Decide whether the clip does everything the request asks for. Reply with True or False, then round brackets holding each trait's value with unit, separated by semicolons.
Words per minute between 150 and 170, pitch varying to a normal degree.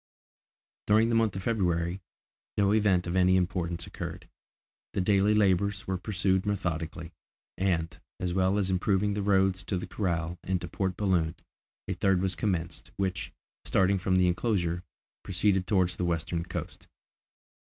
False (155 wpm; 2.1 semitones)